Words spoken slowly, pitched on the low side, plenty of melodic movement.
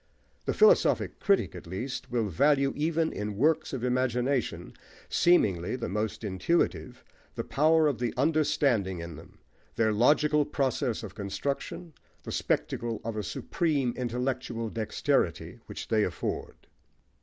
Yes: slow, 130 wpm; low, 125 Hz; wide, 5.8 semitones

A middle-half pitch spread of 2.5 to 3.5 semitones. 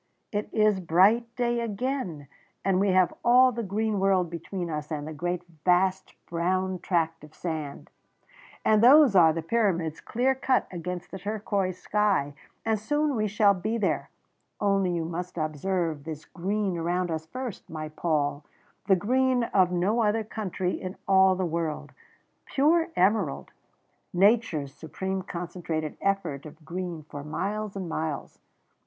No: average, 4.3 semitones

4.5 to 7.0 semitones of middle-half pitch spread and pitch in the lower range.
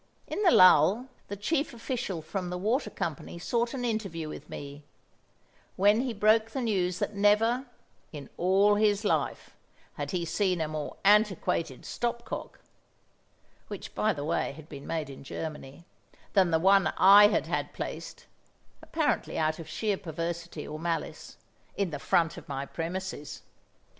No: average, 5.0 semitones; medium, 185 Hz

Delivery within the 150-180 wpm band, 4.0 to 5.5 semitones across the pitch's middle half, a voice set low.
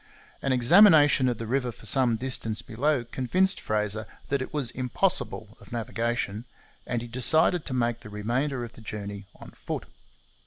No: average, 165 wpm; average, 3.6 semitones; low, 120 Hz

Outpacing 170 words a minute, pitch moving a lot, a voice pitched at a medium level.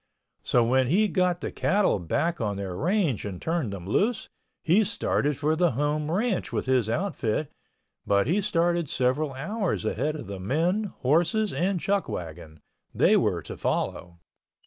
No: average, 160 wpm; wide, 8.0 semitones; medium, 155 Hz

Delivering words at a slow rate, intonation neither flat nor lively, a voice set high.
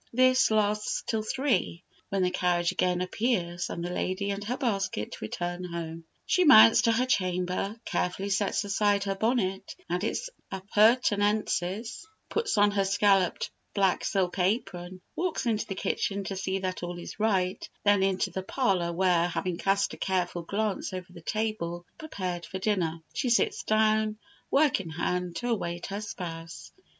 No: average, 160 wpm; average, 3.2 semitones; high, 195 Hz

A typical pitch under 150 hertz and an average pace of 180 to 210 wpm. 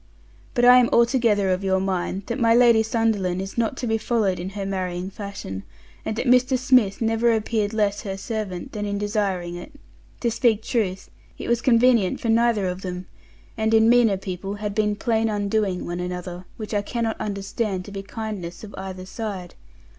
No: high, 210 Hz; average, 190 wpm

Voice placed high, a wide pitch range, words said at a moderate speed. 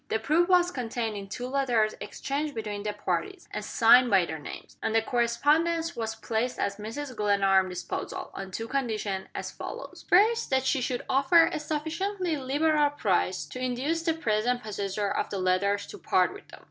Yes: high, 245 Hz; wide, 6.4 semitones; average, 185 wpm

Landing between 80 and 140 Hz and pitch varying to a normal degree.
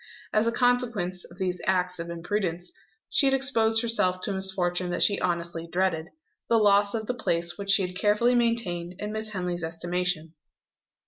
No: high, 190 Hz; average, 3.8 semitones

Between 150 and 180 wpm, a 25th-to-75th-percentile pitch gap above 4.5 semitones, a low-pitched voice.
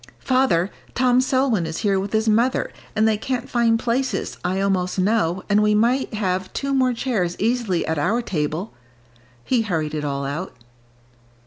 No: average, 165 wpm; average, 5.2 semitones; high, 210 Hz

